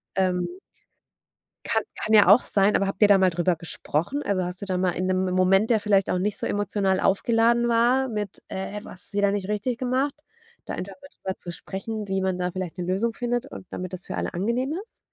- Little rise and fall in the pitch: No, average, 3.5 semitones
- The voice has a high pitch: Yes, high, 195 Hz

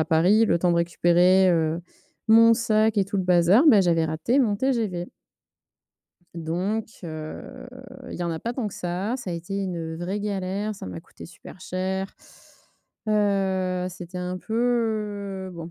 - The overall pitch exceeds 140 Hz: Yes, high, 190 Hz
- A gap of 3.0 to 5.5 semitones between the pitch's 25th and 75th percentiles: Yes, average, 3.5 semitones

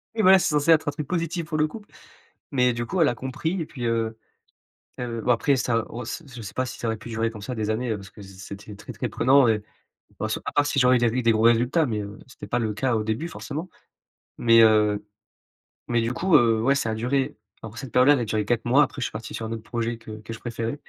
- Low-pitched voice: Yes, low, 120 Hz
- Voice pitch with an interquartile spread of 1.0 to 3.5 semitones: No, average, 3.9 semitones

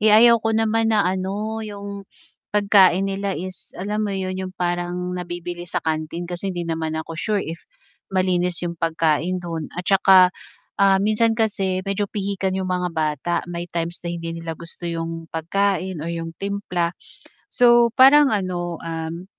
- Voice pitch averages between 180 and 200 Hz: Yes, medium, 185 Hz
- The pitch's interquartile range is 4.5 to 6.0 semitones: No, average, 2.9 semitones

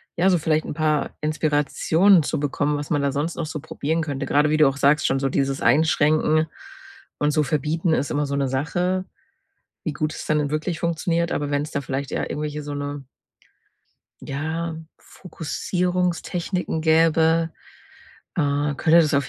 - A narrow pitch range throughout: Yes, narrow, 2.3 semitones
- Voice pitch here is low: No, medium, 155 Hz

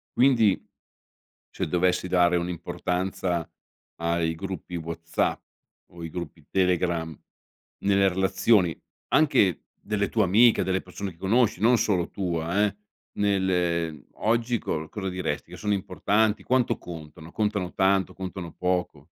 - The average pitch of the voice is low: Yes, very low, 90 Hz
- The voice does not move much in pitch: No, average, 3.0 semitones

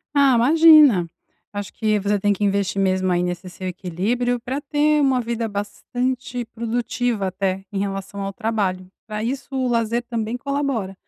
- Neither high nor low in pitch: No, high, 220 Hz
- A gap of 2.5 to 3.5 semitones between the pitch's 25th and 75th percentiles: No, average, 4.1 semitones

